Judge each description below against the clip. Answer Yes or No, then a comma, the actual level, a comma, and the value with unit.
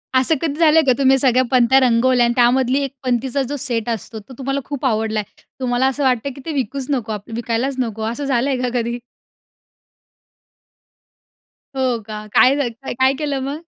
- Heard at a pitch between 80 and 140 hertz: No, very high, 255 Hz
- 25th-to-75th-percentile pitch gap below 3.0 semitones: Yes, narrow, 2.5 semitones